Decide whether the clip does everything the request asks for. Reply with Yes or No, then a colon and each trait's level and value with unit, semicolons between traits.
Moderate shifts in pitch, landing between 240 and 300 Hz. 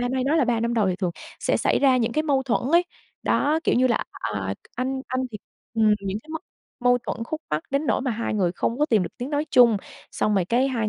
Yes: average, 3.9 semitones; high, 245 Hz